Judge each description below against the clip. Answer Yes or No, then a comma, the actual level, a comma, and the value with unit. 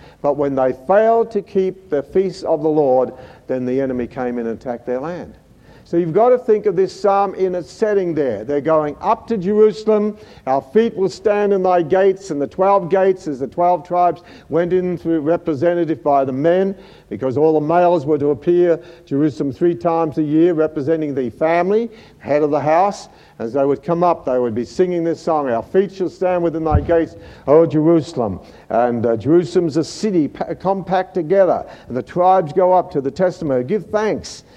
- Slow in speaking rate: No, average, 200 wpm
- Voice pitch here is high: No, medium, 170 Hz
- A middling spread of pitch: Yes, average, 4.6 semitones